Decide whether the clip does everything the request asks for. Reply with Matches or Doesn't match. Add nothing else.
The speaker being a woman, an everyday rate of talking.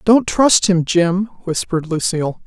Matches